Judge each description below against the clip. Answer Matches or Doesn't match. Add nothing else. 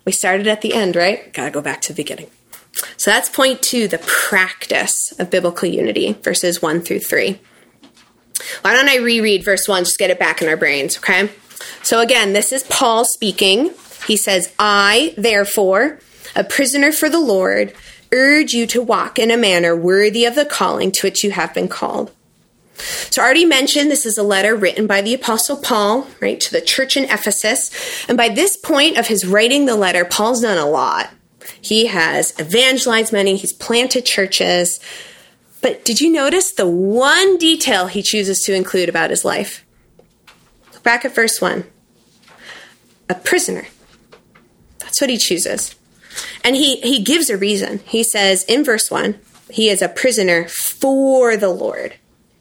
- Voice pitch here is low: Doesn't match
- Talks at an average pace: Matches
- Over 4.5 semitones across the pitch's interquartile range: Matches